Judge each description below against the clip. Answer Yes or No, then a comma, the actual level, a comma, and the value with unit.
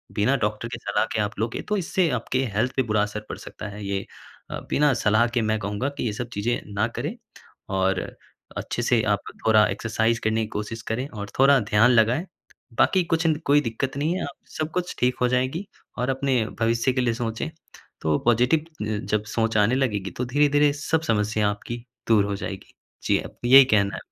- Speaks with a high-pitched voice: No, low, 115 Hz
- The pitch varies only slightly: No, average, 4.2 semitones